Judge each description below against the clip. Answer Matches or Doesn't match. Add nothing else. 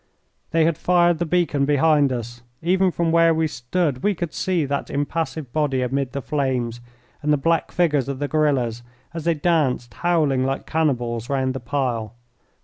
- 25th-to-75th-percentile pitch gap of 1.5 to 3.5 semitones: Doesn't match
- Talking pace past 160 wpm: Matches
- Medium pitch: Matches